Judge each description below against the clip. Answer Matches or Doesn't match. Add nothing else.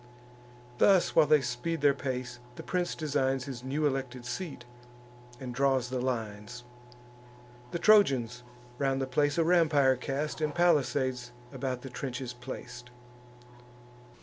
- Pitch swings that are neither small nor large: Matches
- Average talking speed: Doesn't match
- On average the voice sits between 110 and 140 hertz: Matches